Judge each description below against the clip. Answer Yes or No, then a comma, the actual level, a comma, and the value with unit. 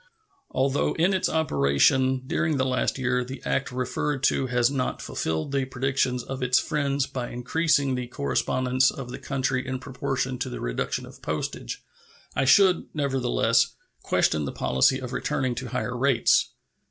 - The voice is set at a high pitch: No, low, 130 Hz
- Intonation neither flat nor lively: No, narrow, 1.7 semitones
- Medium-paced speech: Yes, average, 160 wpm